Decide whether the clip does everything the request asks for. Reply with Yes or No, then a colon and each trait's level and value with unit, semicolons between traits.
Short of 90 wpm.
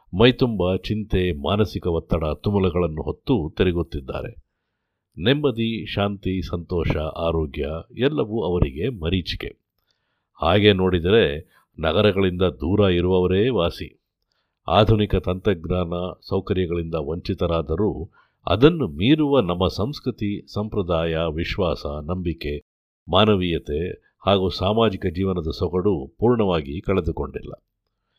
Yes: average, 80 wpm